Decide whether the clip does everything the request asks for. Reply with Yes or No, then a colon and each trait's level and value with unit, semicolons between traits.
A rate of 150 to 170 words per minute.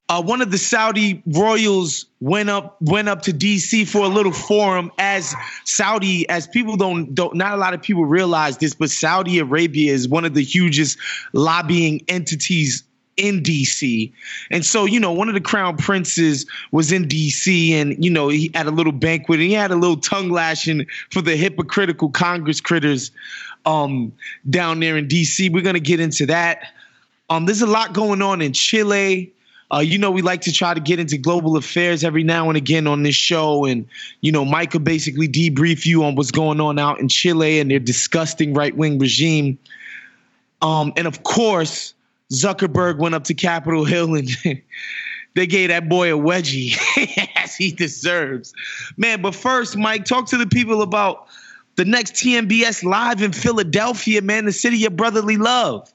No: average, 185 wpm